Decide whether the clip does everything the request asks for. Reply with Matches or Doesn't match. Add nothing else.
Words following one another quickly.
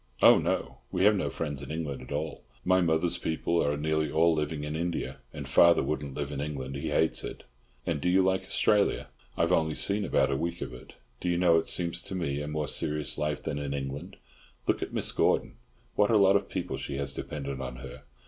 Matches